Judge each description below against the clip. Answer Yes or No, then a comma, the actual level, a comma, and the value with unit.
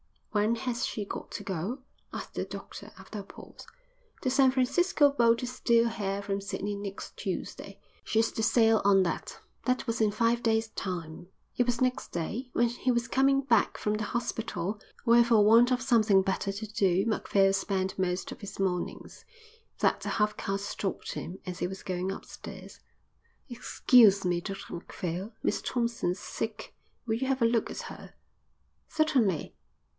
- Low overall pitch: No, high, 220 Hz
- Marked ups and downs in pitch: No, average, 3.6 semitones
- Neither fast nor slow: Yes, average, 170 wpm